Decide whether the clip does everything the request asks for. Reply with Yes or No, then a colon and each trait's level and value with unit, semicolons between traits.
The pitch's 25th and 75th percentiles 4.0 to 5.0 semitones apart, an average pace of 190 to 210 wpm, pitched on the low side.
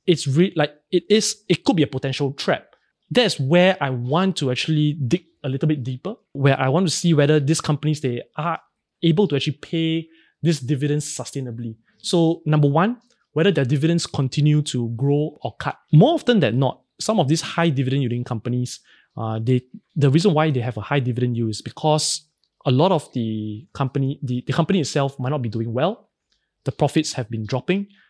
No: average, 4.4 semitones; average, 200 wpm; medium, 150 Hz